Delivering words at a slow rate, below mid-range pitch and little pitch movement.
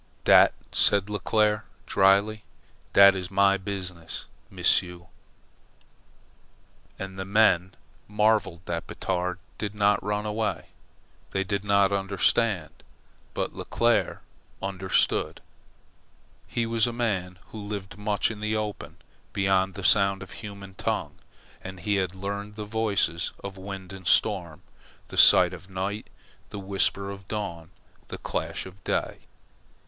Yes: slow, 130 wpm; low, 100 Hz; narrow, 1.8 semitones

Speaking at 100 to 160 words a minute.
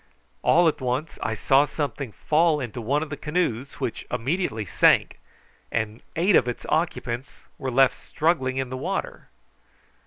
Yes: average, 155 wpm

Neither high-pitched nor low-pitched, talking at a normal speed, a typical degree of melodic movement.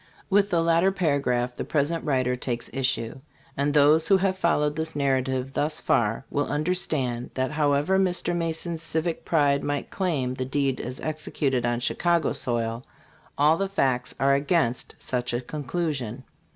Yes: medium, 145 Hz; average, 160 wpm; average, 4.3 semitones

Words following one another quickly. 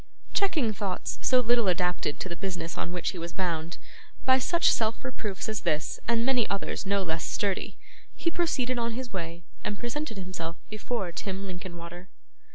No: average, 170 wpm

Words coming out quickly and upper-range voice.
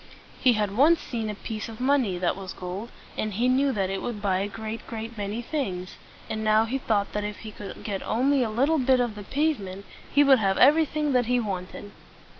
Yes: fast, 225 wpm; high, 220 Hz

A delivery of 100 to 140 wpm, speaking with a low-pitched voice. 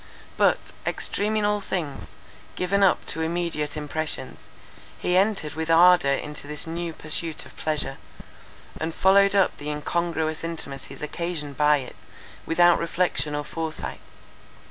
No: slow, 135 wpm; medium, 165 Hz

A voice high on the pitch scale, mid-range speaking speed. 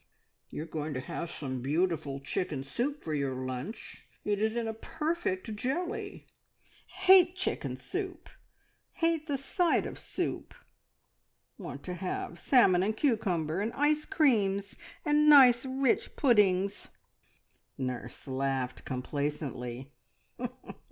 No: high, 200 Hz; slow, 120 wpm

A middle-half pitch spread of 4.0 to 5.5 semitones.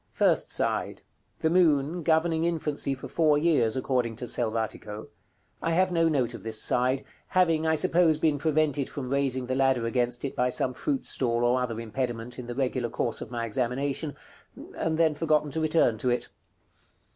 Yes: average, 4.6 semitones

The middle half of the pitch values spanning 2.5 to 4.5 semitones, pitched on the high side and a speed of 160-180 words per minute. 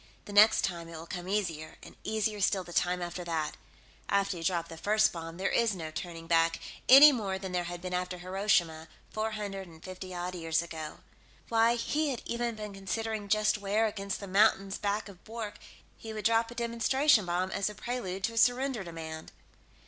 No: average, 4.0 semitones; high, 195 Hz; average, 200 wpm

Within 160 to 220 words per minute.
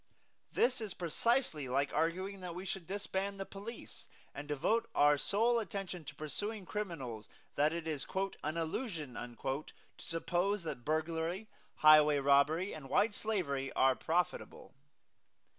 No: slow, 135 wpm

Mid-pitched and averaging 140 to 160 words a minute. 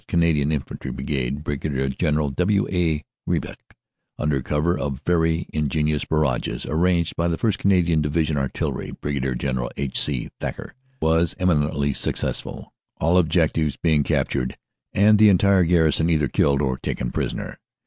No: very low, 75 Hz; average, 150 wpm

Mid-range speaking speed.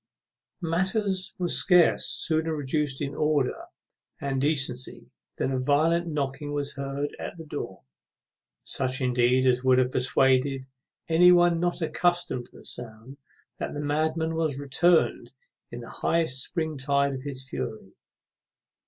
Yes: average, 145 wpm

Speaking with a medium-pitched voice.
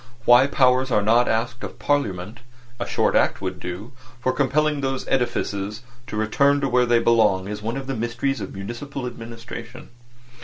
No: low, 120 Hz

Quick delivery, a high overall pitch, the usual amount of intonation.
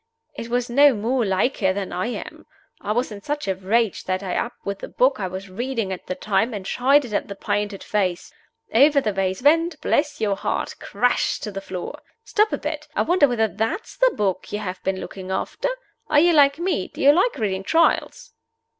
No: fast, 215 wpm; high, 220 Hz; wide, 6.4 semitones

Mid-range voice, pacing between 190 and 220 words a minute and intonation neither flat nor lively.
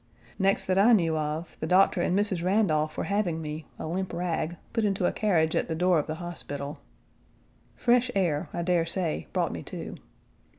Yes: medium, 175 Hz; average, 195 wpm; average, 3.4 semitones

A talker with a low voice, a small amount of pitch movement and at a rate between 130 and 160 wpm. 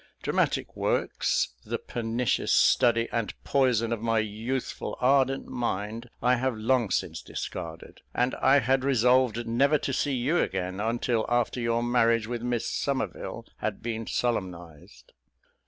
Yes: low, 120 Hz; narrow, 2.2 semitones; average, 140 wpm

